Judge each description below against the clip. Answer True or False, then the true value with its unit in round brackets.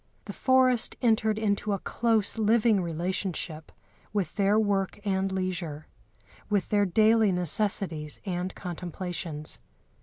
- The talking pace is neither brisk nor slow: False (115 wpm)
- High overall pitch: True (195 Hz)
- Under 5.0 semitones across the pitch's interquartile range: True (3.3 semitones)